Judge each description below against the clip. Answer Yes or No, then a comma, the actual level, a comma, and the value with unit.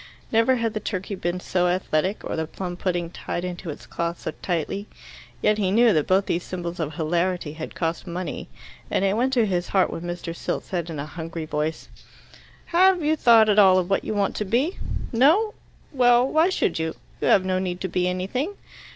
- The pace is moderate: No, fast, 210 wpm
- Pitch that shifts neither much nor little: Yes, average, 4.5 semitones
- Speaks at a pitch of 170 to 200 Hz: Yes, medium, 185 Hz